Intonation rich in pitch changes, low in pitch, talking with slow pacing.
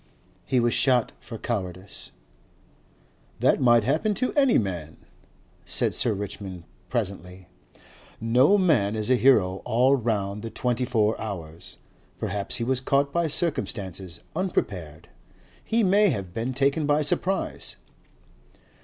Yes: wide, 6.1 semitones; low, 115 Hz; slow, 125 wpm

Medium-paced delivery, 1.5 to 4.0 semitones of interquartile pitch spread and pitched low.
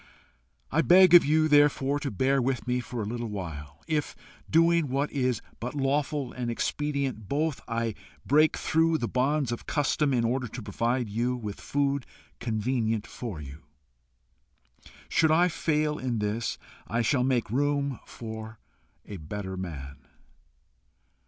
No: average, 145 wpm; average, 4.7 semitones; low, 125 Hz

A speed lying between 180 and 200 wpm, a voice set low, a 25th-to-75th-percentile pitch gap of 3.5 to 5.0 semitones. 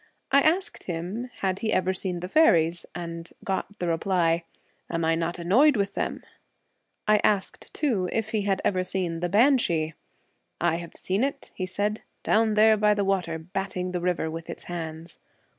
No: average, 190 wpm; medium, 185 Hz; average, 3.8 semitones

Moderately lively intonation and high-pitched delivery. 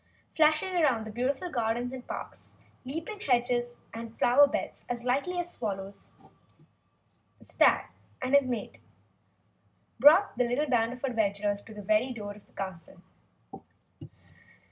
Yes: average, 4.4 semitones; high, 245 Hz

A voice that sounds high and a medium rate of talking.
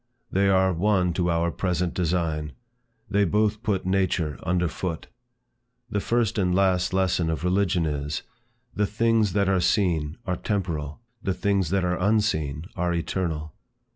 No: very low, 90 Hz; average, 150 wpm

